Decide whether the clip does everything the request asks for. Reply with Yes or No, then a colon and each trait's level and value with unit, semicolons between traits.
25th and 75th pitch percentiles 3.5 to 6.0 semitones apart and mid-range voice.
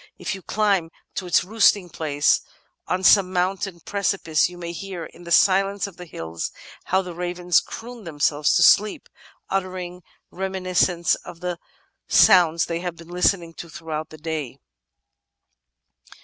No: narrow, 2.5 semitones; medium, 180 Hz